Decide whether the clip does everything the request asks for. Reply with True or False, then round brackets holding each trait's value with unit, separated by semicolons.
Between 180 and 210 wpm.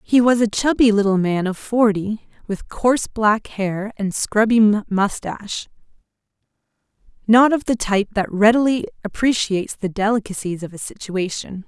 False (140 wpm)